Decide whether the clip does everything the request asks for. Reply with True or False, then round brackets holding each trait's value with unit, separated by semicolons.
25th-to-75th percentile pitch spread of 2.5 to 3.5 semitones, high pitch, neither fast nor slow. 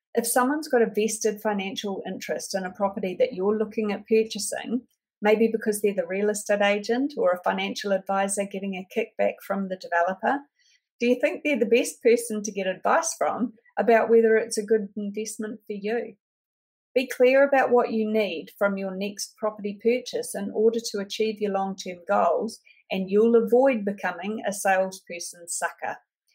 True (2.8 semitones; 215 Hz; 175 wpm)